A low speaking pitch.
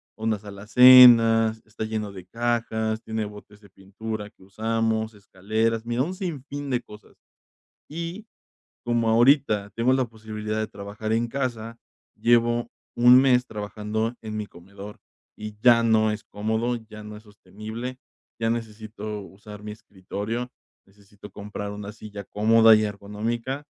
Yes: low, 110 Hz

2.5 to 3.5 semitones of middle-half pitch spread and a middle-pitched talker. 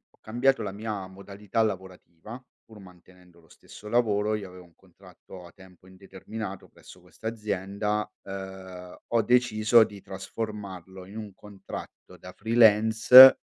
No: average, 2.8 semitones; low, 100 Hz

